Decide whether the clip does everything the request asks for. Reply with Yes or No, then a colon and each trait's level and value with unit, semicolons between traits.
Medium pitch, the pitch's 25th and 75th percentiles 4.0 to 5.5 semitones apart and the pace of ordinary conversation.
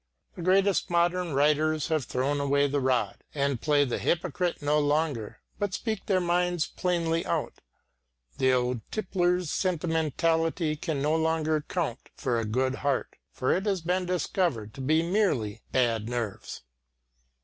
Yes: medium, 155 Hz; average, 4.7 semitones; average, 150 wpm